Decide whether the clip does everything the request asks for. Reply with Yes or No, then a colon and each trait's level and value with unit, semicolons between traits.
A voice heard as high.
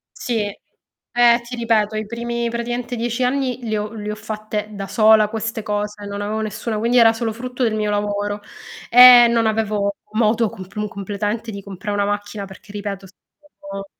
Yes: high, 215 Hz